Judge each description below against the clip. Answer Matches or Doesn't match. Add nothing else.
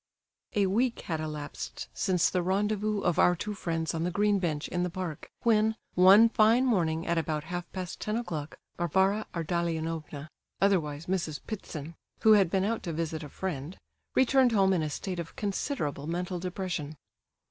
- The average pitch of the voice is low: Doesn't match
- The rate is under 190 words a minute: Matches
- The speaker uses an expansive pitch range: Doesn't match